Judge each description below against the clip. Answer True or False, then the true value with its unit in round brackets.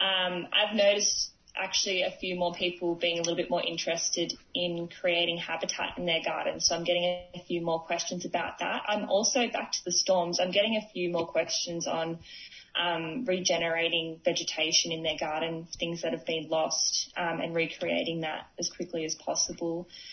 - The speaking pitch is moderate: True (170 Hz)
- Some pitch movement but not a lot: False (1.3 semitones)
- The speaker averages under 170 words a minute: False (180 wpm)